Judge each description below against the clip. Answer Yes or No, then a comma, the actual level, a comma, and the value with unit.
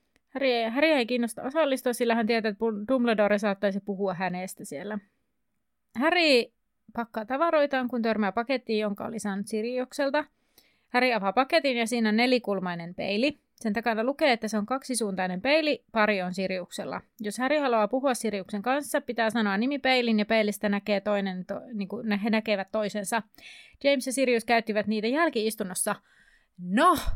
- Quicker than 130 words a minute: Yes, average, 150 wpm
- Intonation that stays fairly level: No, average, 3.9 semitones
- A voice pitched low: No, high, 230 Hz